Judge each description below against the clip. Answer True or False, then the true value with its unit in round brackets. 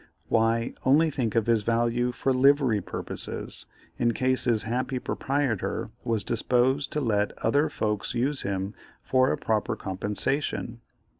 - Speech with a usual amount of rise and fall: True (3.0 semitones)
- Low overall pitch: True (120 Hz)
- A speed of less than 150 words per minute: True (140 wpm)